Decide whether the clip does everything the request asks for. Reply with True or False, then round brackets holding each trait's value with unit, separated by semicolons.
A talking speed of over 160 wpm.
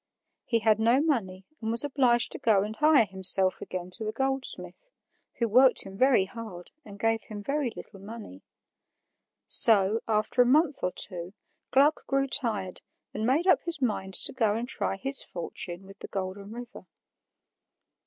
True (170 wpm)